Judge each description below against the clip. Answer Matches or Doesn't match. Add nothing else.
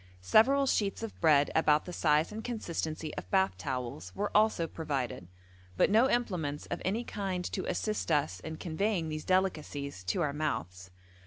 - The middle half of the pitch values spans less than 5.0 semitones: Doesn't match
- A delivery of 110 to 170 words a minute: Matches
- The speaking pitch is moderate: Matches